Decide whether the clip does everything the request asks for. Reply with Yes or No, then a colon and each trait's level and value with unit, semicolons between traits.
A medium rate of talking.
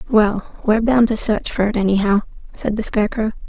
Yes: average, 190 wpm